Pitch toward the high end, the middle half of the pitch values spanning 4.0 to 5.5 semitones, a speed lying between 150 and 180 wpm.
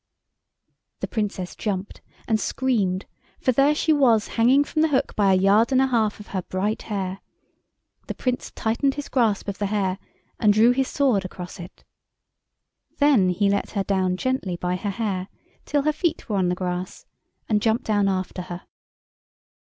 Yes: high, 210 Hz; average, 5.1 semitones; average, 175 wpm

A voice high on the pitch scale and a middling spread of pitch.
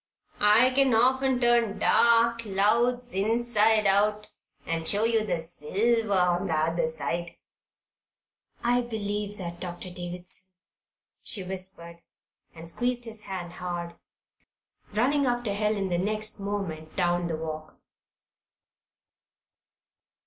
Yes: high, 205 Hz; average, 4.8 semitones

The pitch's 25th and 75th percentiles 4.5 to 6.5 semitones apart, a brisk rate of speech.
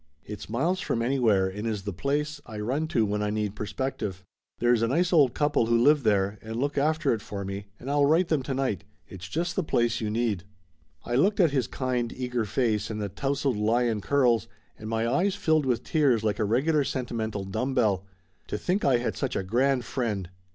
Yes: average, 4.9 semitones; fast, 220 wpm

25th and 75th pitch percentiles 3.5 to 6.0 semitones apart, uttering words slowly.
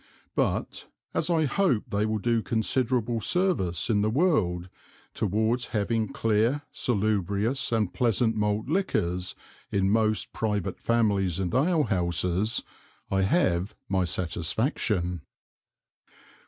Yes: average, 4.0 semitones; slow, 110 wpm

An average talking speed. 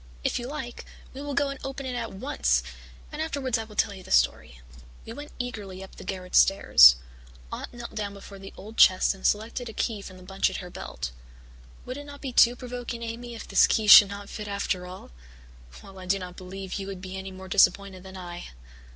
No: fast, 225 wpm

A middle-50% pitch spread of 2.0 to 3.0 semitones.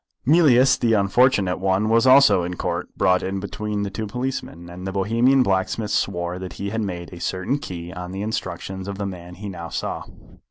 No: average, 3.7 semitones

